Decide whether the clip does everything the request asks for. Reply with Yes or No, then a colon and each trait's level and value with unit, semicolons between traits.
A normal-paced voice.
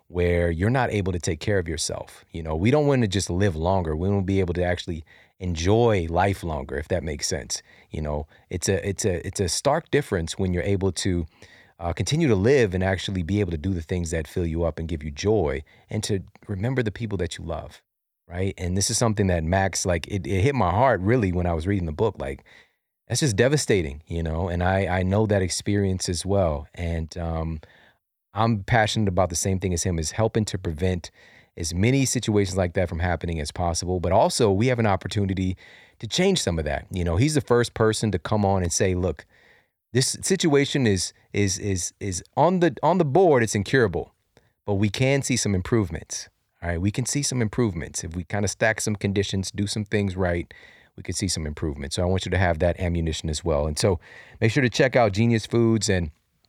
No: fast, 230 wpm